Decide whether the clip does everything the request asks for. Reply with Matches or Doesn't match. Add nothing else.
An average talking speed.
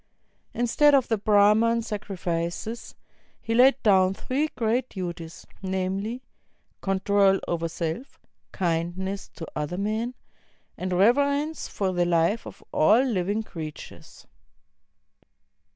Doesn't match